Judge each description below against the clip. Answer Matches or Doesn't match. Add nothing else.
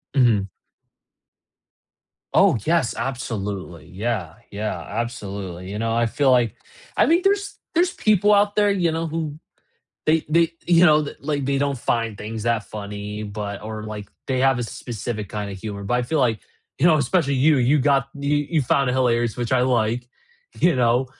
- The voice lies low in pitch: Matches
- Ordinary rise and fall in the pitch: Doesn't match